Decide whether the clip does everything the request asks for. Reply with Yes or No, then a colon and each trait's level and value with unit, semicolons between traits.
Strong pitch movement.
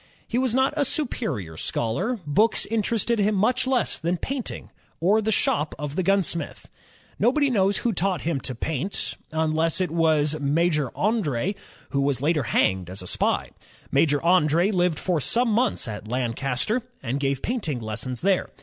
Yes: wide, 7.6 semitones